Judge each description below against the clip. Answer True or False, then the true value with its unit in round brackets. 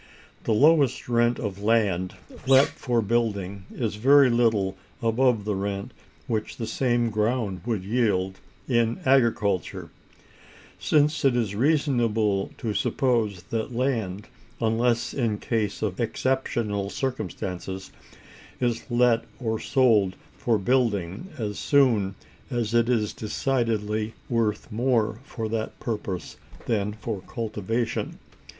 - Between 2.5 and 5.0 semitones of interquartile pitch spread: True (2.9 semitones)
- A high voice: False (115 Hz)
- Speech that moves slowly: True (120 wpm)